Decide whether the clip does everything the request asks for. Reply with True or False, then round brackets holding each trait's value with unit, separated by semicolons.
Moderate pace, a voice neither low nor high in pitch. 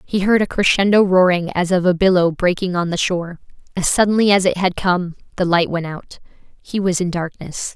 False (210 wpm; 180 Hz)